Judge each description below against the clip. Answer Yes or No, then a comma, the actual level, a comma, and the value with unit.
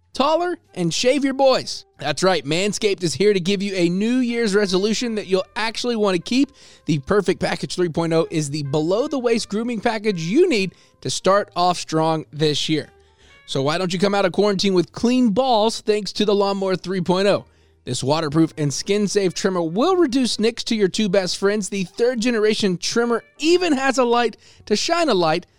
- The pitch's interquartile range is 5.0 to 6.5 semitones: Yes, average, 5.3 semitones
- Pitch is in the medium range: No, high, 200 Hz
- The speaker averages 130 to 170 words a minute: No, average, 195 wpm